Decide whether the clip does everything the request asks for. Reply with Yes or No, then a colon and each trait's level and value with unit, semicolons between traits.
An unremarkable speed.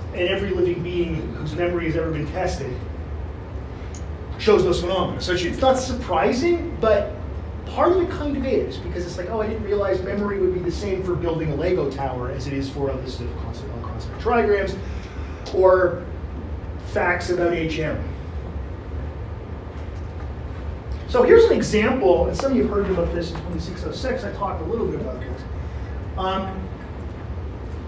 Yes: average, 160 wpm